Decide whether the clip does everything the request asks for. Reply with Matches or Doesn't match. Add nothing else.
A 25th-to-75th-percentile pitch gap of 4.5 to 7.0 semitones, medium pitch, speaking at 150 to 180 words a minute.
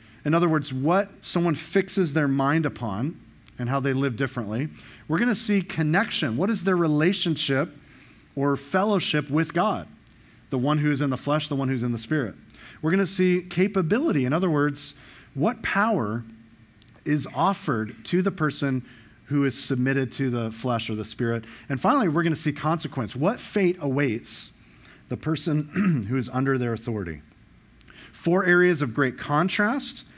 Matches